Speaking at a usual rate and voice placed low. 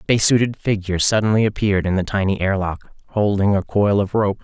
Yes: average, 190 wpm; low, 100 Hz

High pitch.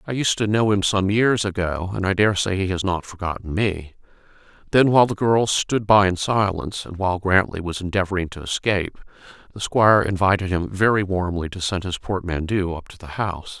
No: very low, 95 Hz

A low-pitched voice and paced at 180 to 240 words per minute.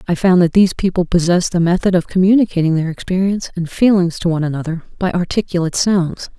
No: medium, 180 Hz; average, 190 wpm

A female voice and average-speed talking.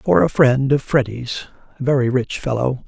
No: male; average, 165 wpm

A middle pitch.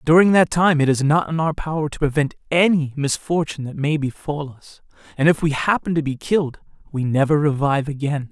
Yes: medium, 150 Hz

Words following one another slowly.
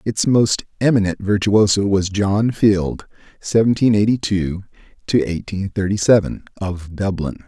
Yes: slow, 130 wpm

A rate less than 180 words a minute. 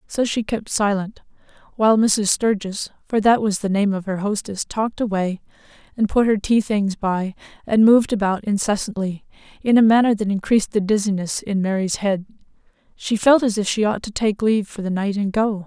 No: average, 195 wpm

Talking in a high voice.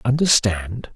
No: low, 120 Hz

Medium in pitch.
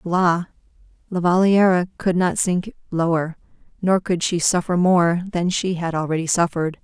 Yes: medium, 175 Hz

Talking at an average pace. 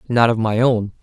No: fast, 235 wpm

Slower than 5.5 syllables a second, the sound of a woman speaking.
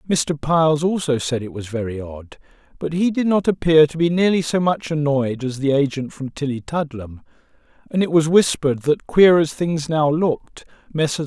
No: 4.9 syllables/s; male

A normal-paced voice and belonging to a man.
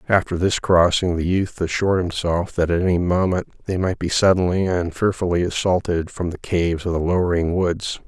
Yes: average, 185 wpm; male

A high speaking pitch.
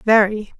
Yes: high, 210 Hz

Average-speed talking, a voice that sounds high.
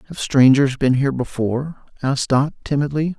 No: average, 150 wpm; low, 135 Hz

